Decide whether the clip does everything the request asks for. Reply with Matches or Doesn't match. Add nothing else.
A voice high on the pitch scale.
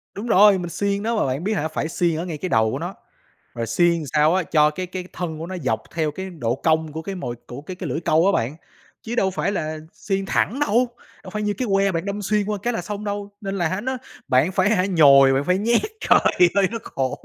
Doesn't match